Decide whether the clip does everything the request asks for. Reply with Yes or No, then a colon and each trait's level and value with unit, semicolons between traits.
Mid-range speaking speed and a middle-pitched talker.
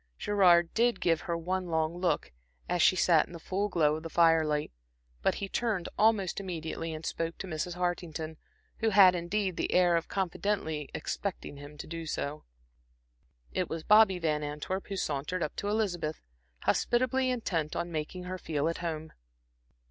Yes: average, 170 wpm; medium, 170 Hz